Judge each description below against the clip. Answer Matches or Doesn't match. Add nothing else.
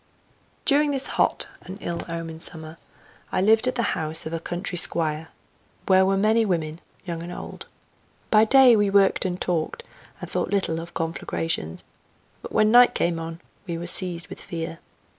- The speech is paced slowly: Doesn't match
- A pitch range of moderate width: Matches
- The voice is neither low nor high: Matches